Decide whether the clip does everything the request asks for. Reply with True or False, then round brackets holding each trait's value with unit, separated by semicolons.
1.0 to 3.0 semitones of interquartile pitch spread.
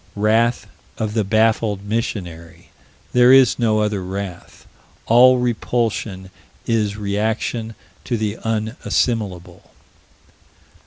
True (2.5 semitones)